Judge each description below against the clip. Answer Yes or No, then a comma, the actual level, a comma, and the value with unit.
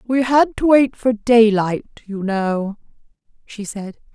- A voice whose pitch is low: No, high, 225 Hz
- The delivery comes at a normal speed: Yes, average, 145 wpm